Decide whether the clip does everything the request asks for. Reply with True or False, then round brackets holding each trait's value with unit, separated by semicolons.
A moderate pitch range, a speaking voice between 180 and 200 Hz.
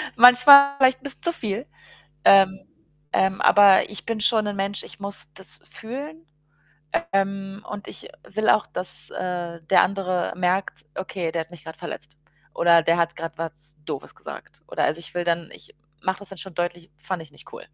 True (3.3 semitones; 190 Hz)